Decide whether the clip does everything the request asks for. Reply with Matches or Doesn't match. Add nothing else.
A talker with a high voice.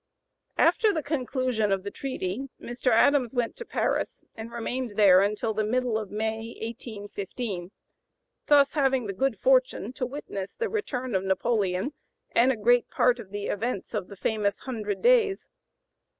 Matches